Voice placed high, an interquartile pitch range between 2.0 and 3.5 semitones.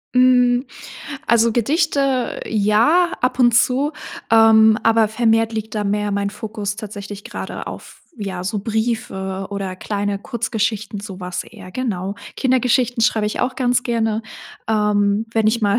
Yes: high, 220 Hz; average, 2.8 semitones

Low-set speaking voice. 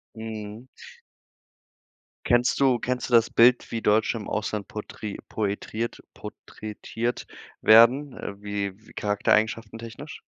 Yes: low, 110 Hz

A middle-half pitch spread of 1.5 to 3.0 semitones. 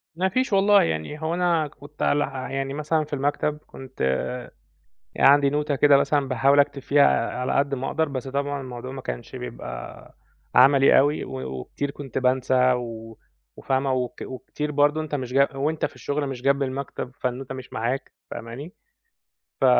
Yes: narrow, 2.4 semitones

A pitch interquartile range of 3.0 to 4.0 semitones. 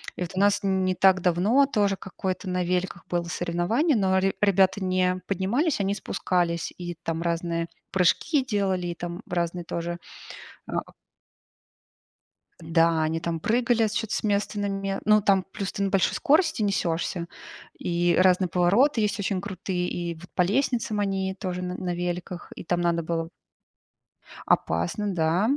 No: narrow, 2.6 semitones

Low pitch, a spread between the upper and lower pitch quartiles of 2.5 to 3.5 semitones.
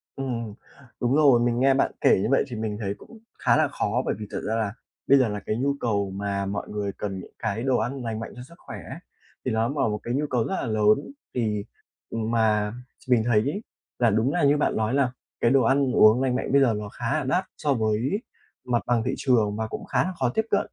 No: low, 120 Hz; average, 3.9 semitones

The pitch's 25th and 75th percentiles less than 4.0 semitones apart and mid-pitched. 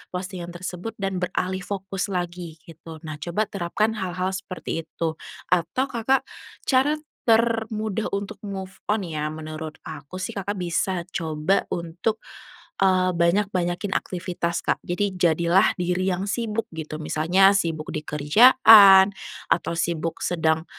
Yes: average, 3.1 semitones; medium, 180 Hz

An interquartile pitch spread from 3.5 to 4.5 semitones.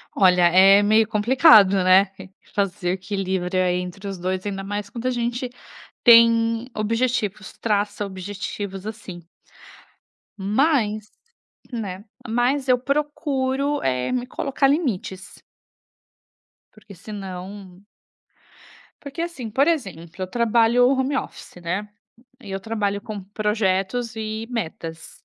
Yes: average, 4.1 semitones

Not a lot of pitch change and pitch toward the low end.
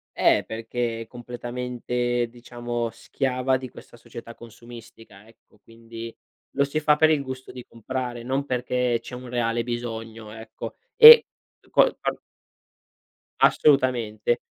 Yes: narrow, 1.7 semitones; low, 120 Hz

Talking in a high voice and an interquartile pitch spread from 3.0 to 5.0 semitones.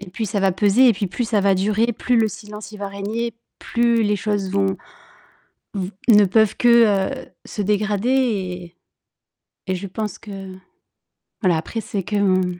No: high, 205 Hz; narrow, 2.6 semitones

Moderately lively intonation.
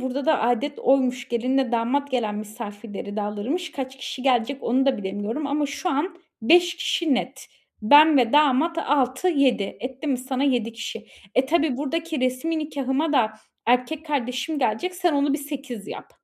Yes: average, 3.4 semitones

